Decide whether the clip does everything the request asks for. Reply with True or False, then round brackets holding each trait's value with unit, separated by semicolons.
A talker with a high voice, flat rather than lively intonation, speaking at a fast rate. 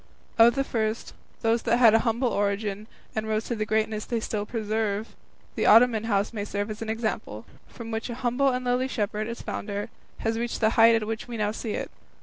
True (225 Hz; 1.6 semitones; 215 wpm)